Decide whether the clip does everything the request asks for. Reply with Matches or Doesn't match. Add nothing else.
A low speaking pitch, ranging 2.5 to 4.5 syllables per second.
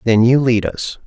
Matches